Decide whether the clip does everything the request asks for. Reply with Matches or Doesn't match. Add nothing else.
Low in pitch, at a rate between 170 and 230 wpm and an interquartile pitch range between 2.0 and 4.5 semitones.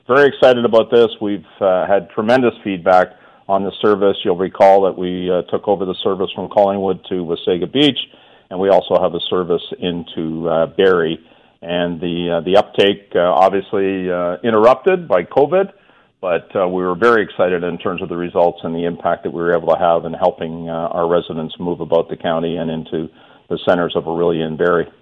Matches